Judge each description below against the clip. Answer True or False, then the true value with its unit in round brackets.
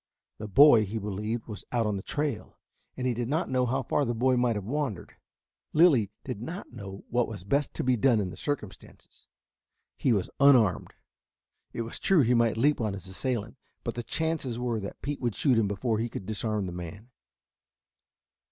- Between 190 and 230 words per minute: True (200 wpm)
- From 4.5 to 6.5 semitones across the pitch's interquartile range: False (3.7 semitones)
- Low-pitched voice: True (115 Hz)